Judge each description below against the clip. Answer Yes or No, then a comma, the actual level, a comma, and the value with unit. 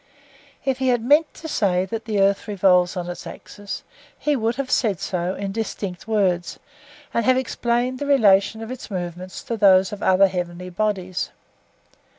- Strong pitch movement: No, average, 4.3 semitones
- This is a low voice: No, high, 200 Hz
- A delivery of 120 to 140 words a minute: No, average, 175 wpm